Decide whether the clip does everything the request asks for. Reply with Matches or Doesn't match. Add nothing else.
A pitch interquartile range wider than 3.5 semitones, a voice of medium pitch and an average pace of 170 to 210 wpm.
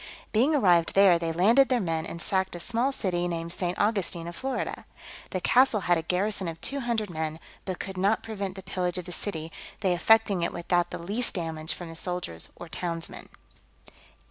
Matches